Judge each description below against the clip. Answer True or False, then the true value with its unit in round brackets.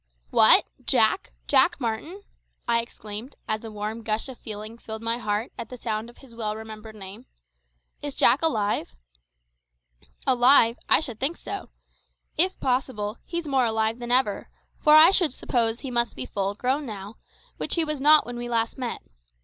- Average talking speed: True (175 wpm)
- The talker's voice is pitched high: True (235 Hz)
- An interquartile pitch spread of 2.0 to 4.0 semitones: True (3.5 semitones)